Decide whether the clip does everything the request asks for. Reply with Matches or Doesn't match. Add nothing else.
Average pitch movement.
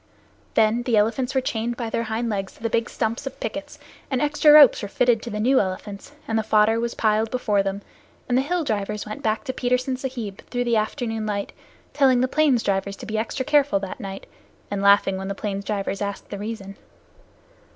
Matches